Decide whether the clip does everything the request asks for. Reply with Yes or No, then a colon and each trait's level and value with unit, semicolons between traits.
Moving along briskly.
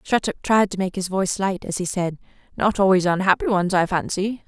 Yes: fast, 215 wpm